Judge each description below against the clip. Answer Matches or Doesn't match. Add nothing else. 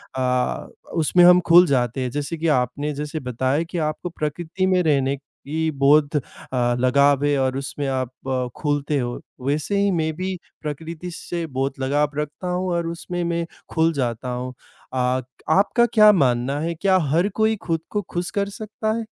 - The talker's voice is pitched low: Doesn't match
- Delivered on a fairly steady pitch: Doesn't match